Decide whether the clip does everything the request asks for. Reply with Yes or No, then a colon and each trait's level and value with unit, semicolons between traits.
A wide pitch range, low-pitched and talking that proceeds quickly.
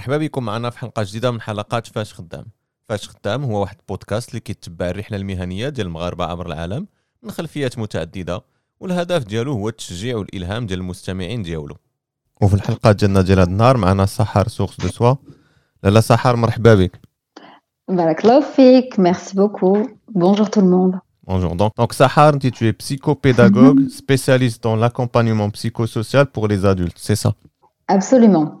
Yes: wide, 5.8 semitones; low, 115 Hz; fast, 155 wpm